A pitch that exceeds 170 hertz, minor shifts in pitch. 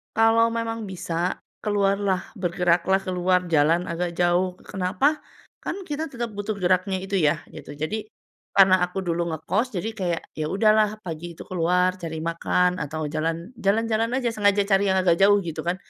No: medium, 185 Hz; average, 3.5 semitones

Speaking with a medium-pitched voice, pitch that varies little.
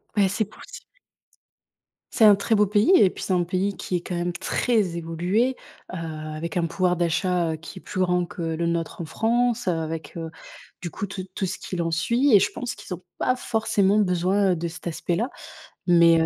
No: medium, 180 Hz; average, 3.5 semitones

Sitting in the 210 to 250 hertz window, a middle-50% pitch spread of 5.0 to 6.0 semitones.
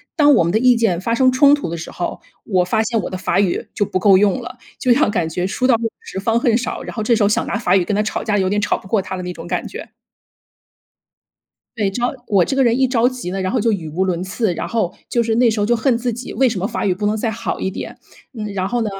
No: high, 215 Hz; average, 4.1 semitones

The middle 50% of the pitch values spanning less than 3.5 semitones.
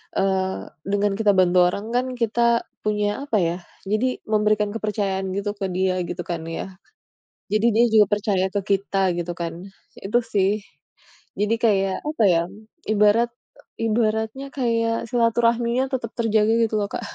Yes: average, 3.1 semitones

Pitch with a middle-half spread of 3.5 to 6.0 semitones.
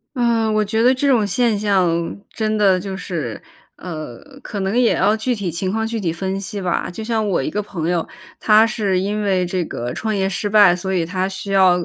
No: average, 3.1 semitones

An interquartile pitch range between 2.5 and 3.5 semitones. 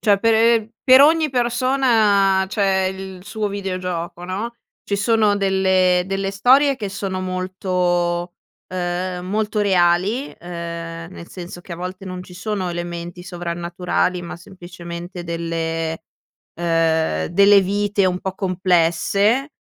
Yes: average, 2.8 semitones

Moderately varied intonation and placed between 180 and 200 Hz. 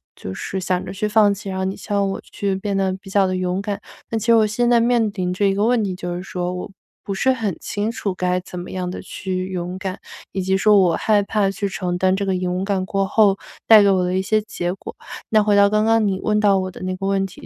No: narrow, 2.1 semitones; high, 195 Hz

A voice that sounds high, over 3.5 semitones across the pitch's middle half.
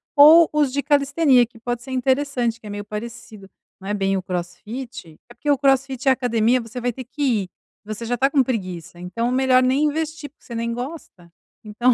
Yes: high, 245 Hz; average, 3.9 semitones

